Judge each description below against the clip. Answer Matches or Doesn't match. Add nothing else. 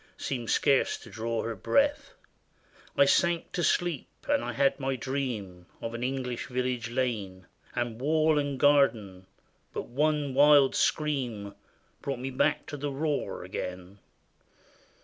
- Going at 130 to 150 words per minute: Matches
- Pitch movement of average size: Matches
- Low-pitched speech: Matches